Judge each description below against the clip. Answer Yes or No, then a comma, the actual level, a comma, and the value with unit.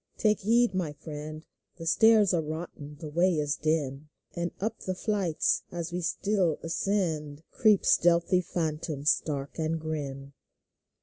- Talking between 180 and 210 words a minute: No, average, 140 wpm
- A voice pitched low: No, medium, 165 Hz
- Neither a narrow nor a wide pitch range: Yes, average, 3.6 semitones